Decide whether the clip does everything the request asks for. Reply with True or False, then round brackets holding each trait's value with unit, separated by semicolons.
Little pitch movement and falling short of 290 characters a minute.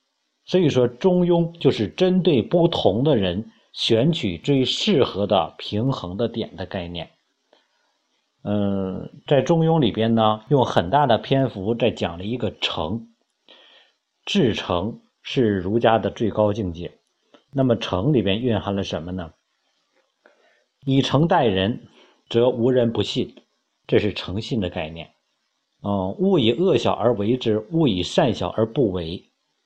False (5.4 semitones; 195 characters per minute)